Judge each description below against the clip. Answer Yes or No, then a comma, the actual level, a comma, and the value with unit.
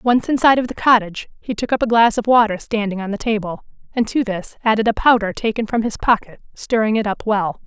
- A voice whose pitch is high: Yes, high, 220 Hz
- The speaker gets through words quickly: Yes, fast, 235 wpm